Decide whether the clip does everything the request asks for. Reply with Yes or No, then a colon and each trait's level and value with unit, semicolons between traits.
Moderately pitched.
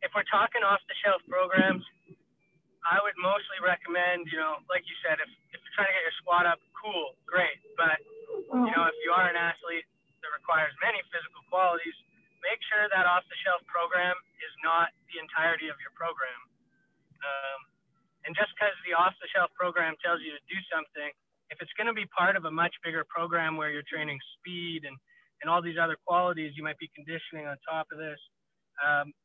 Yes: medium, 170 Hz